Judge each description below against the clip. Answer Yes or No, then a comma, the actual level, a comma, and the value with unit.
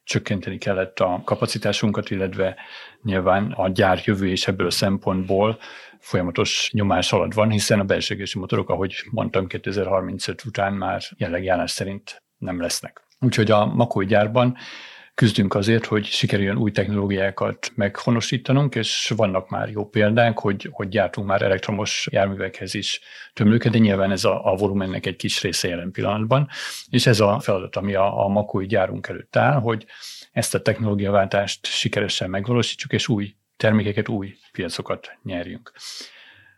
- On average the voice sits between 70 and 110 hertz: Yes, low, 105 Hz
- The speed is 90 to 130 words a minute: No, average, 145 wpm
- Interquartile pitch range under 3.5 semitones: Yes, narrow, 2.6 semitones